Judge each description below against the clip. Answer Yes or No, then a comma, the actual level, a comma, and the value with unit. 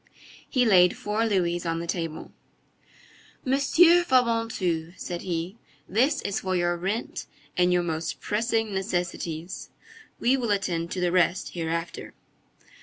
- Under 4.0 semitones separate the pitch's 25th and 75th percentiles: No, average, 4.7 semitones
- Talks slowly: Yes, slow, 130 wpm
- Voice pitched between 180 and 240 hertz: Yes, medium, 185 Hz